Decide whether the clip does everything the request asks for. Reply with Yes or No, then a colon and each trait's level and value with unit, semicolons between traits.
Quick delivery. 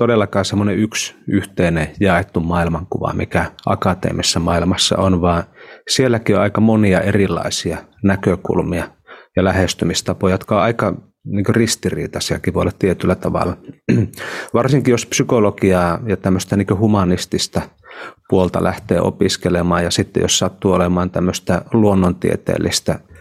No: average, 115 wpm